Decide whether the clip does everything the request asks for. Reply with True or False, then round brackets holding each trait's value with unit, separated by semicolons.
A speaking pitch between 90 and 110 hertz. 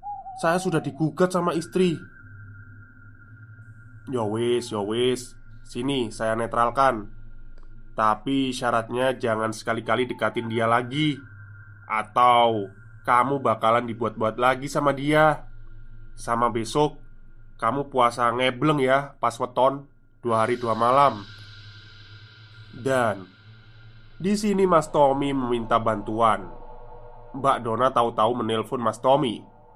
False (120 Hz)